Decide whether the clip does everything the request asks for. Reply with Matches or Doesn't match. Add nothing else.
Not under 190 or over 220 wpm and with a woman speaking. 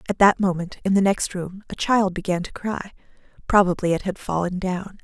Matches